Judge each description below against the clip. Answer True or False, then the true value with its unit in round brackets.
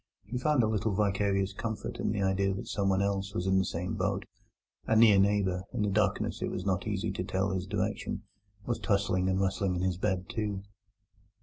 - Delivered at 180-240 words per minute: True (205 wpm)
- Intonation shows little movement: True (1.6 semitones)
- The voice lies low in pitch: True (100 Hz)